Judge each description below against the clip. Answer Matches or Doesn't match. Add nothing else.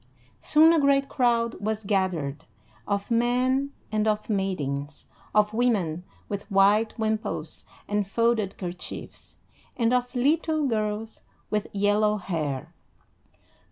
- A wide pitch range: Doesn't match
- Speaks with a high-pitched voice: Matches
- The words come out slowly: Matches